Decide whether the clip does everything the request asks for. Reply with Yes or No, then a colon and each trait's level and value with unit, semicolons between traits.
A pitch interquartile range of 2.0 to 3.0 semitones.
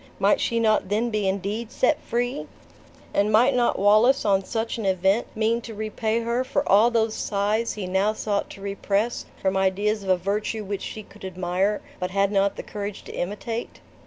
Yes: narrow, 2.6 semitones